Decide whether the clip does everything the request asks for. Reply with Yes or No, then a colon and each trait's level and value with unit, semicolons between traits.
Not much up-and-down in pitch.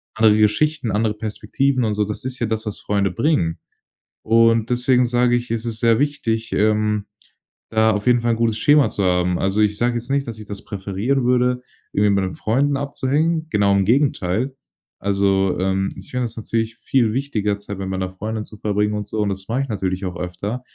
No: average, 3.4 semitones